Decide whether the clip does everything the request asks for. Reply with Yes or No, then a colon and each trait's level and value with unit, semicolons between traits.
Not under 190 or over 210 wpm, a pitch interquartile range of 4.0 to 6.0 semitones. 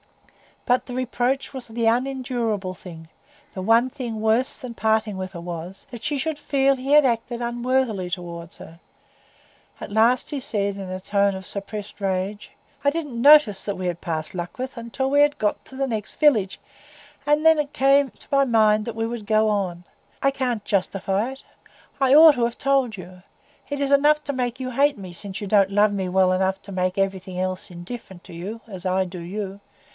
Yes: average, 200 wpm; wide, 5.5 semitones